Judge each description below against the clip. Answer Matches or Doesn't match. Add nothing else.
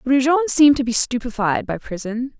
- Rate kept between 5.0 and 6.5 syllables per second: Matches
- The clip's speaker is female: Matches